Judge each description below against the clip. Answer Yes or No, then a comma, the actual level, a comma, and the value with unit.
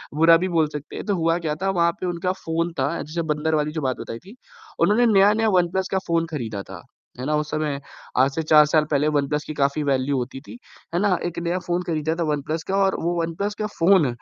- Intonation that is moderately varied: Yes, average, 3.0 semitones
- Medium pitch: Yes, medium, 160 Hz